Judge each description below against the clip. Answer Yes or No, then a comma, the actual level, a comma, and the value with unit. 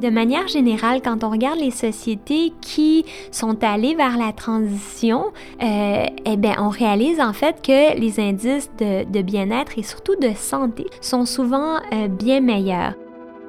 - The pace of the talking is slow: No, average, 160 wpm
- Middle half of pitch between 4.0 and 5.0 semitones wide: Yes, average, 4.4 semitones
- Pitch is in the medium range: No, high, 235 Hz